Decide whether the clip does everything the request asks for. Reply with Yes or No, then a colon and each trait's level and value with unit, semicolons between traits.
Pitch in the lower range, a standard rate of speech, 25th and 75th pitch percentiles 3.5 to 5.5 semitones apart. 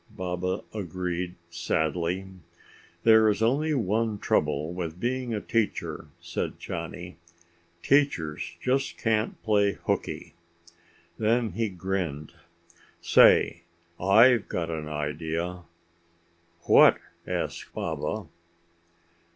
No: very low, 95 Hz; slow, 95 wpm; average, 4.6 semitones